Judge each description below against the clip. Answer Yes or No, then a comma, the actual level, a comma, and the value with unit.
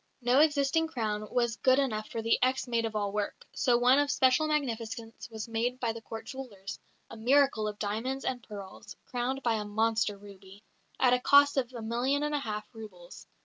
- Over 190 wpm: Yes, average, 200 wpm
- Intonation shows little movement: No, average, 3.5 semitones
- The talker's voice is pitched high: Yes, high, 235 Hz